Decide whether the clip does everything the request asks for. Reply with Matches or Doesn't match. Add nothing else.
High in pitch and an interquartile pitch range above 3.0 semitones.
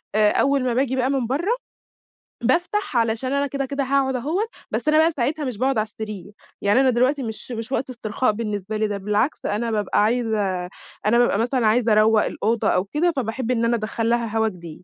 Matches